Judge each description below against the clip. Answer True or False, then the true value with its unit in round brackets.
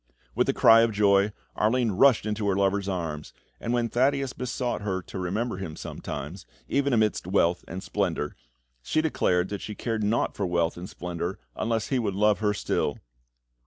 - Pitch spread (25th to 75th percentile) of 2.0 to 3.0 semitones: False (4.0 semitones)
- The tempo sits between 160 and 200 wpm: True (180 wpm)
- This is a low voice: True (105 Hz)